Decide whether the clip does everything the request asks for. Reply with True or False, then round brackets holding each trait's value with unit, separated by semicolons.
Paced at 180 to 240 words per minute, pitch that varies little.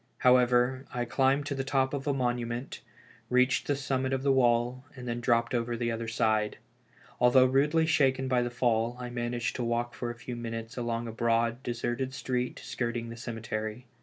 True (190 wpm; 1.9 semitones)